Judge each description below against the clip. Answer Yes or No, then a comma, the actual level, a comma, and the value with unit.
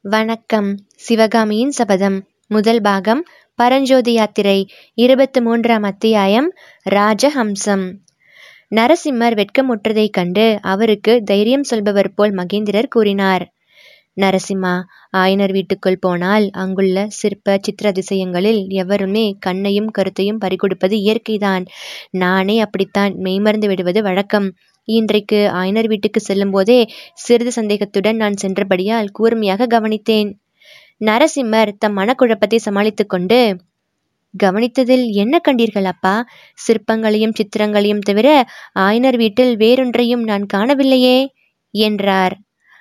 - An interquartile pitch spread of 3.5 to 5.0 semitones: No, average, 2.8 semitones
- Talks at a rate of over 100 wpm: No, average, 95 wpm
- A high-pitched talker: Yes, high, 210 Hz